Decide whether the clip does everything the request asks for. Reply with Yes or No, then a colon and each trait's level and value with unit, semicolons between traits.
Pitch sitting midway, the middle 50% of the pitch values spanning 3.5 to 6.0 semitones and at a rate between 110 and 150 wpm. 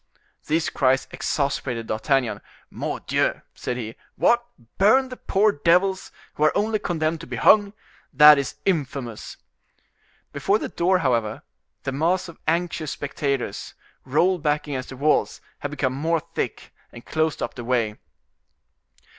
Yes: medium, 150 Hz; average, 5.1 semitones; average, 140 wpm